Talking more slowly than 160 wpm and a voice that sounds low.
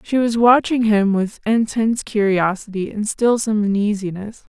No: average, 145 wpm; high, 215 Hz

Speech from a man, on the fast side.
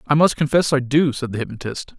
Yes: male; fast, 240 wpm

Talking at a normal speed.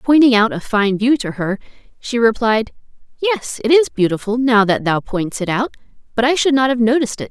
No: fast, 215 wpm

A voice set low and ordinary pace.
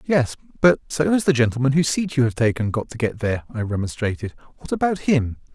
No: low, 125 Hz; fast, 215 wpm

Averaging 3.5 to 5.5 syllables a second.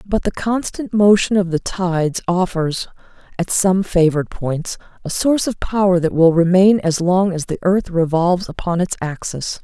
Yes: 4.8 syllables/s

